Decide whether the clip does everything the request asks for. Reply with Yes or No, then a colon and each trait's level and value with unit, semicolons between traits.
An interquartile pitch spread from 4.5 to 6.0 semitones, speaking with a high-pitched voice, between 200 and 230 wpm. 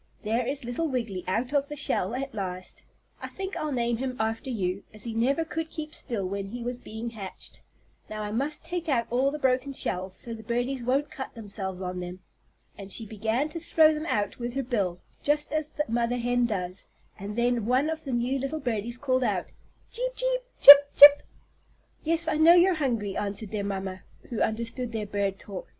Yes: average, 5.3 semitones; high, 240 Hz; fast, 205 wpm